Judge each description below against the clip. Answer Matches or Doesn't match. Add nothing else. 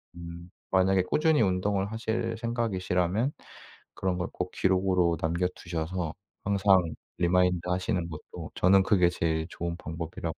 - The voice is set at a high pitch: Doesn't match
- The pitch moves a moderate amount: Doesn't match